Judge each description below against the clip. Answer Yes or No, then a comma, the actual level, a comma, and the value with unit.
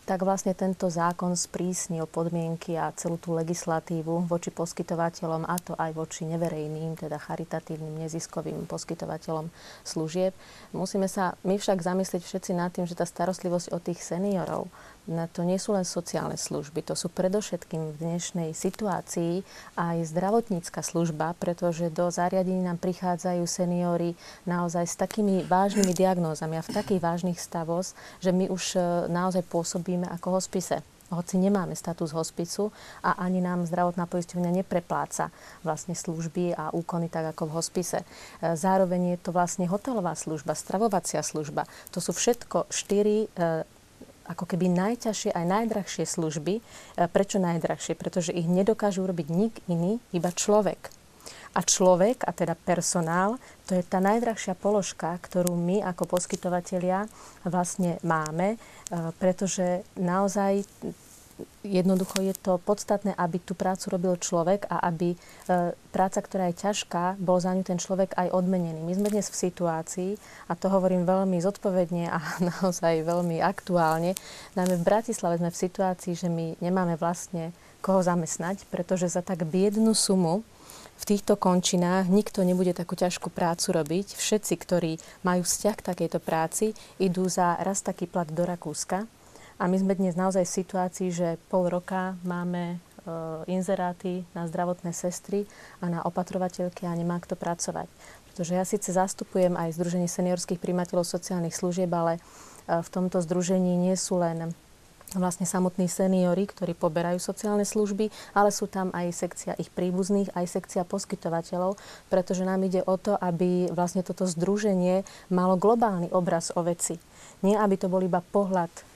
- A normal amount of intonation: No, narrow, 1.8 semitones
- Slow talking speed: No, average, 145 wpm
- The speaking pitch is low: No, medium, 180 Hz